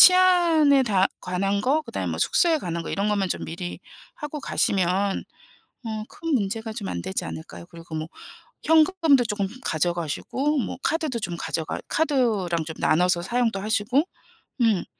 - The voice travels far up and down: Yes, wide, 8.2 semitones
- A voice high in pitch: Yes, high, 210 Hz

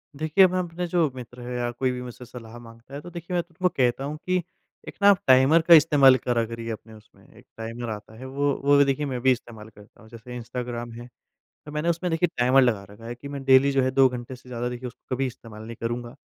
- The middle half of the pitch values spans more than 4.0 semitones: No, average, 3.3 semitones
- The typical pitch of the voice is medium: No, low, 125 Hz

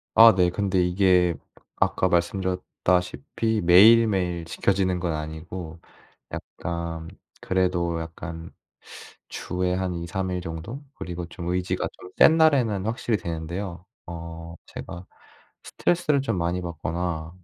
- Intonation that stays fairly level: Yes, narrow, 2.1 semitones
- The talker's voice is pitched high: No, very low, 90 Hz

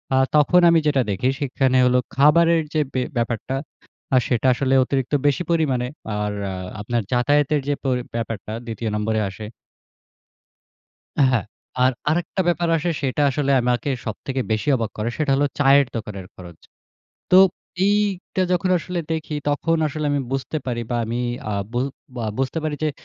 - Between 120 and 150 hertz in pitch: Yes, low, 135 Hz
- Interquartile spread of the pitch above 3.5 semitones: Yes, average, 4.6 semitones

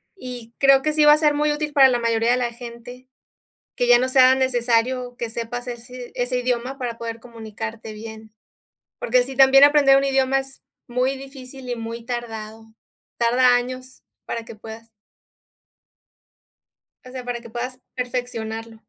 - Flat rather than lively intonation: Yes, narrow, 2.1 semitones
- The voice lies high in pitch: Yes, high, 245 Hz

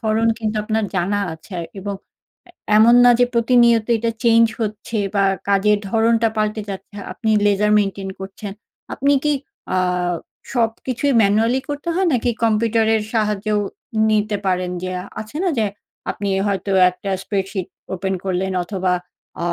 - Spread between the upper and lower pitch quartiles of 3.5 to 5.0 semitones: No, narrow, 2.6 semitones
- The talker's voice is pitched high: Yes, high, 215 Hz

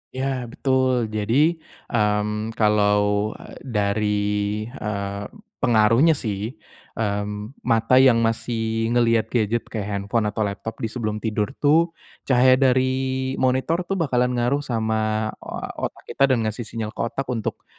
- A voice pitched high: No, low, 115 Hz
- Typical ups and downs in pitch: Yes, average, 3.2 semitones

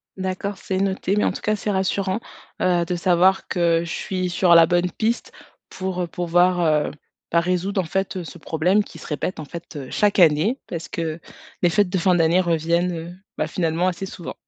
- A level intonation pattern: Yes, narrow, 2.0 semitones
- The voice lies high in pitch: No, medium, 180 Hz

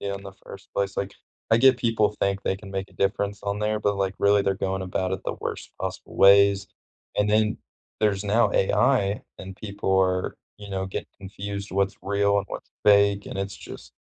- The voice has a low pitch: Yes, low, 100 Hz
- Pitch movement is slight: Yes, narrow, 1.1 semitones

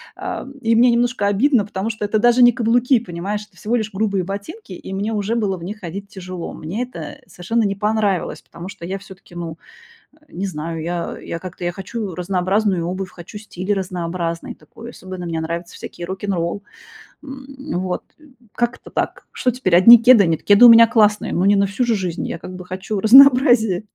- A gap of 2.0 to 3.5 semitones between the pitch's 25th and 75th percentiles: No, average, 4.1 semitones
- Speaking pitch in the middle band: No, high, 200 Hz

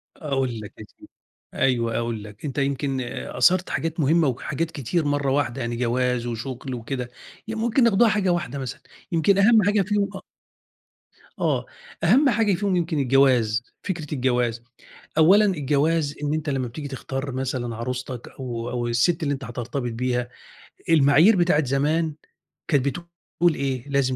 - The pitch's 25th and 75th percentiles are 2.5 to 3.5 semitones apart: No, average, 5.0 semitones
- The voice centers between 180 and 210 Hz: No, medium, 140 Hz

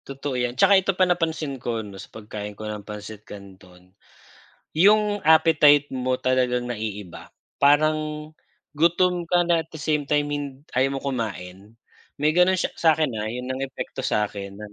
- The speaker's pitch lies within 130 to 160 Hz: Yes, low, 135 Hz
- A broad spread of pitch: Yes, wide, 6.6 semitones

